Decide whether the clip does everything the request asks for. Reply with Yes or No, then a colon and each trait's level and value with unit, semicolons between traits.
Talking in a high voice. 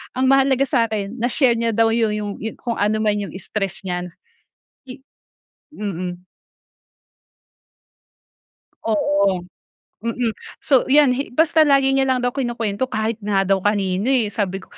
Yes: high, 225 Hz